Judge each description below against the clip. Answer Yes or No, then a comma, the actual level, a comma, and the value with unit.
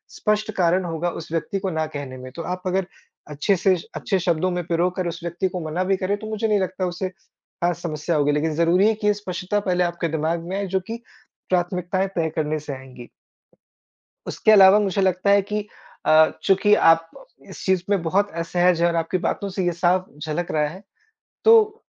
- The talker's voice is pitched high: No, medium, 180 Hz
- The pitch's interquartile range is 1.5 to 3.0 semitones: Yes, average, 2.7 semitones